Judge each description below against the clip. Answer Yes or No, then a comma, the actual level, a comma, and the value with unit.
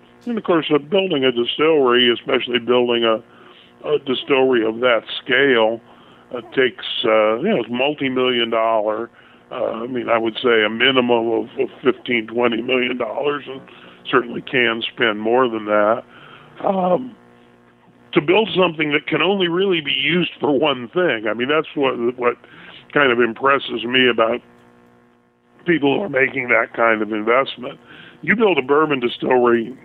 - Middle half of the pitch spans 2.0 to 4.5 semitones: Yes, average, 3.8 semitones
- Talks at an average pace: Yes, average, 160 wpm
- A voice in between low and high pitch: No, low, 120 Hz